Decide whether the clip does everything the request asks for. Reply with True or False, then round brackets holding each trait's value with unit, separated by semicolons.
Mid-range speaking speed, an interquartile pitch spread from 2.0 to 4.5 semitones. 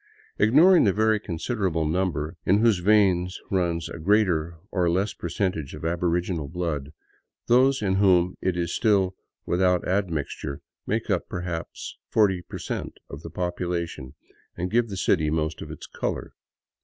True (150 wpm; 3.3 semitones)